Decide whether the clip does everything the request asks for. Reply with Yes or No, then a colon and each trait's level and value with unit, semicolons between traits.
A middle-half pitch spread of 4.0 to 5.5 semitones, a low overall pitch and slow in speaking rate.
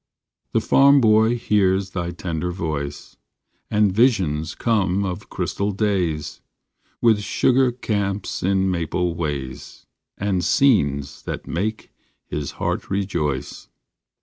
Yes: average, 4.8 semitones; very low, 95 Hz; slow, 110 wpm